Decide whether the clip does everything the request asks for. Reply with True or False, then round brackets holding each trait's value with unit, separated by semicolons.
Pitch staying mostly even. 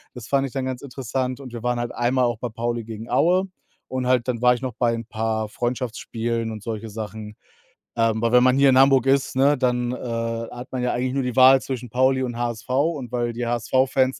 True (2.0 semitones)